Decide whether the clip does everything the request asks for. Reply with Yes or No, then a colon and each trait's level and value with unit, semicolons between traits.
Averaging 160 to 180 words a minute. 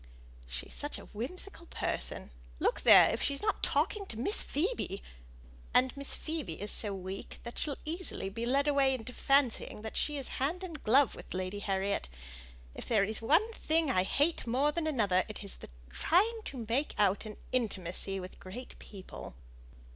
Yes: average, 170 wpm